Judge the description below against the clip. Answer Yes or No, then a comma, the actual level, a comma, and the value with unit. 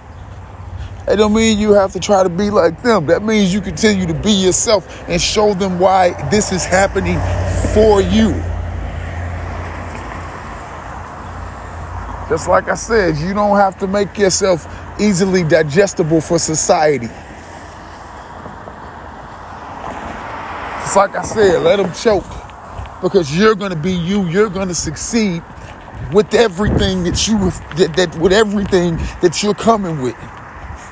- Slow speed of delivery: Yes, slow, 130 wpm